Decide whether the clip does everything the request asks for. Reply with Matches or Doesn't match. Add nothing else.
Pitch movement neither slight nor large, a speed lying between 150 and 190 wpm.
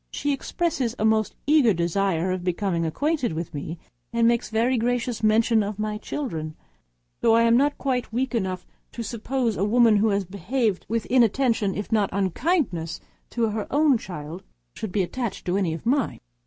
Matches